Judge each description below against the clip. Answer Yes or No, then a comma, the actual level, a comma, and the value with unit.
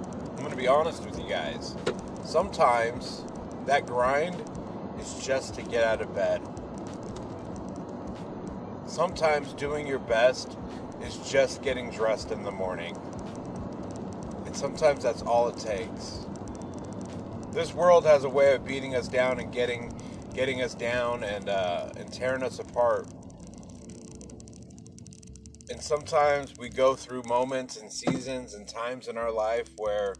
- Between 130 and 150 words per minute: Yes, slow, 135 wpm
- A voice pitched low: Yes, low, 125 Hz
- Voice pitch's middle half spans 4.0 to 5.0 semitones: No, narrow, 2.6 semitones